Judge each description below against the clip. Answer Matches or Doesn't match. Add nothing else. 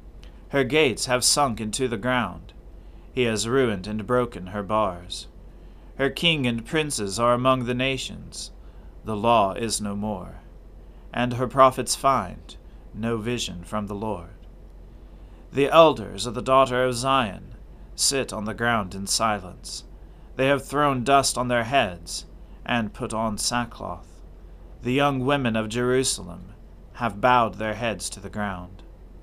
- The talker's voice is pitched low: Matches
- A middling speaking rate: Matches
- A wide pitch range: Matches